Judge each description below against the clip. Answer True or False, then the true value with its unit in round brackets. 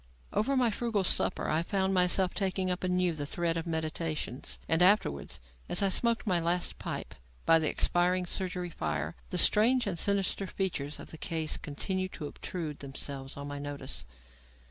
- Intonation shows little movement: False (3.7 semitones)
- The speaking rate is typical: True (175 wpm)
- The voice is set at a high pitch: False (175 Hz)